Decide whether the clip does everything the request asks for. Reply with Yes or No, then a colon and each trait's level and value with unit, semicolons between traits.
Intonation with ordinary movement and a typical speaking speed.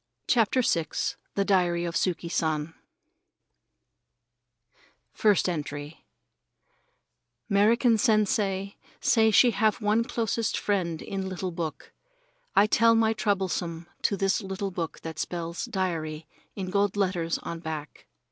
No: average, 4.0 semitones; slow, 120 wpm